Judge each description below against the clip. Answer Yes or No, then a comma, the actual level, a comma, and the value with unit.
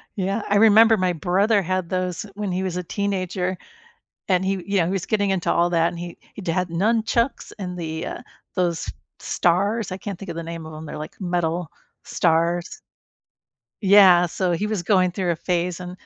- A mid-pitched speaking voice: Yes, medium, 180 Hz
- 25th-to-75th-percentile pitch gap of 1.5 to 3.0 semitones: Yes, narrow, 2.5 semitones